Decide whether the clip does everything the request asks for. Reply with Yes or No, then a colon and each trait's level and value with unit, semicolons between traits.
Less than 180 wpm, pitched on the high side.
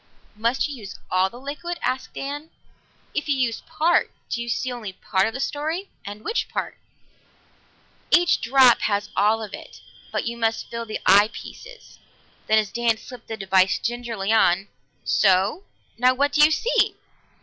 Yes: average, 170 wpm; high, 235 Hz